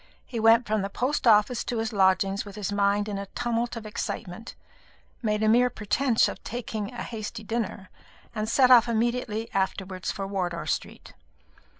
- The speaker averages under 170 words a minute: No, average, 175 wpm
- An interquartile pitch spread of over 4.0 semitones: No, average, 2.8 semitones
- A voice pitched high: Yes, high, 215 Hz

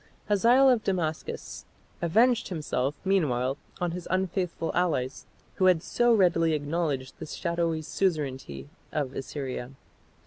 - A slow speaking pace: Yes, slow, 115 wpm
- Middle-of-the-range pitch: Yes, medium, 165 Hz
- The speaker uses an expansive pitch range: No, average, 4.8 semitones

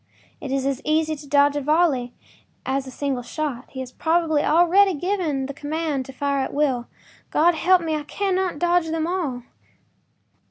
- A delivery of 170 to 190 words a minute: Yes, average, 175 wpm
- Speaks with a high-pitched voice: Yes, very high, 300 Hz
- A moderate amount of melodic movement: Yes, average, 3.6 semitones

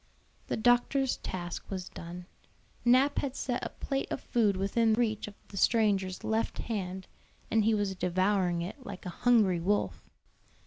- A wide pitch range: No, average, 4.2 semitones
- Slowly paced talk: No, average, 160 wpm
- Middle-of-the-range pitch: No, high, 205 Hz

